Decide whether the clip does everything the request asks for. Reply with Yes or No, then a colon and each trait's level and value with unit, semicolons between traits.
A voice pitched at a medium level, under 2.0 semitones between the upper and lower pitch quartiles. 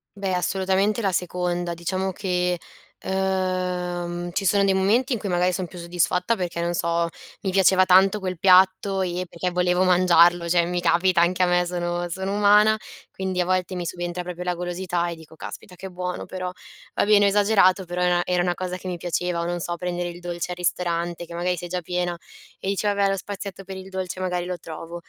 Yes: medium, 180 Hz; narrow, 1.4 semitones